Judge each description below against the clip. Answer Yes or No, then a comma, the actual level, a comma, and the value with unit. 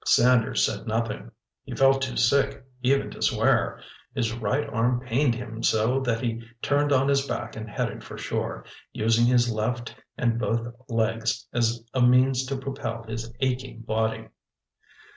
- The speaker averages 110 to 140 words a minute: No, average, 160 wpm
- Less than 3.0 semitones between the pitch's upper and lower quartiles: Yes, narrow, 2.4 semitones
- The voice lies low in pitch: Yes, low, 120 Hz